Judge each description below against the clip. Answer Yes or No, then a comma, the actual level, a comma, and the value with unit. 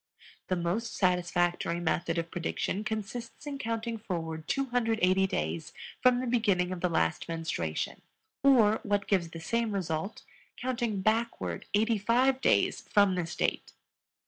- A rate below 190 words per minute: Yes, average, 140 wpm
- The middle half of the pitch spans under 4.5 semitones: No, average, 5.1 semitones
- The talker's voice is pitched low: No, high, 200 Hz